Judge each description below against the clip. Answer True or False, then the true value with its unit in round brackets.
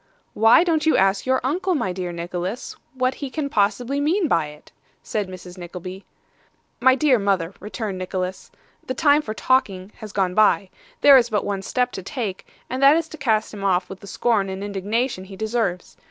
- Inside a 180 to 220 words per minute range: True (195 wpm)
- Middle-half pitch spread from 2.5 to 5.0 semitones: False (5.5 semitones)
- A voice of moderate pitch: False (210 Hz)